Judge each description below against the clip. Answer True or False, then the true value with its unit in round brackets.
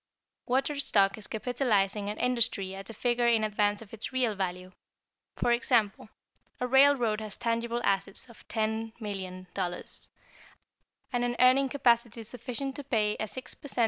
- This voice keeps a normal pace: True (150 wpm)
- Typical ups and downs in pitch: True (3.3 semitones)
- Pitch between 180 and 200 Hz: False (225 Hz)